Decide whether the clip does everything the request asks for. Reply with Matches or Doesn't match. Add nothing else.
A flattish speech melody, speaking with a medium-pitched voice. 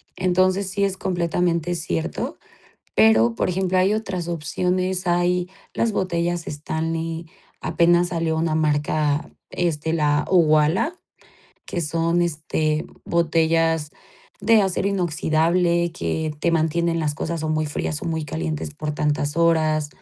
Matches